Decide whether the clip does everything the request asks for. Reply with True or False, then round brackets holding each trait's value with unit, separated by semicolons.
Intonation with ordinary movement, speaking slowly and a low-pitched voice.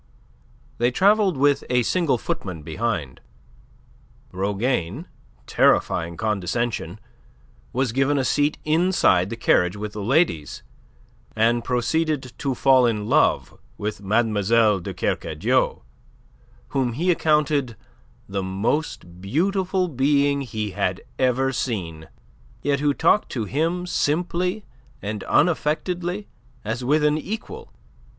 False (6.6 semitones; 115 wpm; 125 Hz)